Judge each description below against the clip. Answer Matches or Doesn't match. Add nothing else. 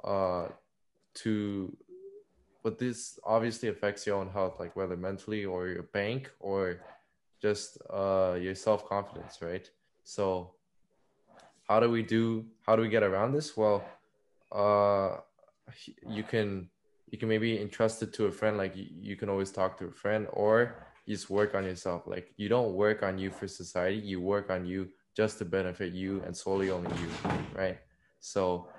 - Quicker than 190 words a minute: Doesn't match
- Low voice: Matches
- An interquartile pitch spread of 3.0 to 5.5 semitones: Doesn't match